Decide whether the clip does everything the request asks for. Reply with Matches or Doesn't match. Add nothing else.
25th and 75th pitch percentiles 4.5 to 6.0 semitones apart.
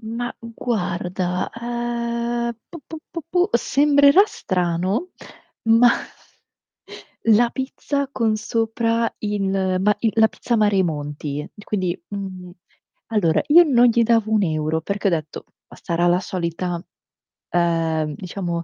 Matches